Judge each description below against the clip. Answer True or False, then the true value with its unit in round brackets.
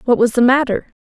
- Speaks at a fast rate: True (235 wpm)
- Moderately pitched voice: False (245 Hz)